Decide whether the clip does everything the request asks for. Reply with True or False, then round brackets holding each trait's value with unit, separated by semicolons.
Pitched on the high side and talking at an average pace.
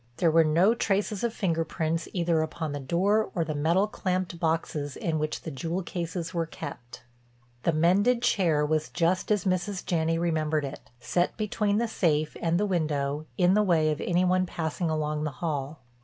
False (165 Hz; 185 wpm)